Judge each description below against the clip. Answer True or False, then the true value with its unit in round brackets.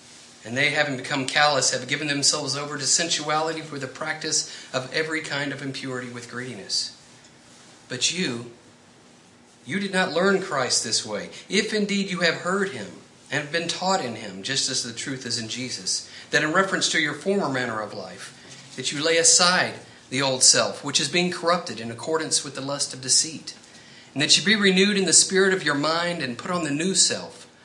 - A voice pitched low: False (145 Hz)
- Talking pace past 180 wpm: True (200 wpm)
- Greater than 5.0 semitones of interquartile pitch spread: True (5.4 semitones)